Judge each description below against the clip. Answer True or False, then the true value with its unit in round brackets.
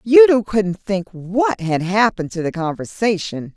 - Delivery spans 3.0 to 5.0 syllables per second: True (4.4 syllables/s)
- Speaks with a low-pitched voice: False (200 Hz)